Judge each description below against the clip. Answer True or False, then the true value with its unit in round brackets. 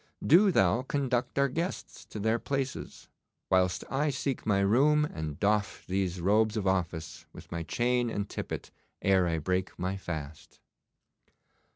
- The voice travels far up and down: True (6.0 semitones)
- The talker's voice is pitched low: True (100 Hz)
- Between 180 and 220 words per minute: False (150 wpm)